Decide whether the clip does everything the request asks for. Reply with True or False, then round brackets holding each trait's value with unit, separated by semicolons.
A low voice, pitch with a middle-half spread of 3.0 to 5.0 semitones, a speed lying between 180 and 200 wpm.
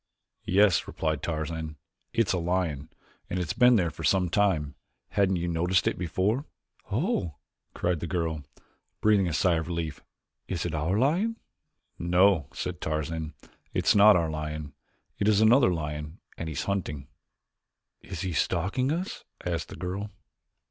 False (85 Hz; 4.1 semitones; 160 wpm)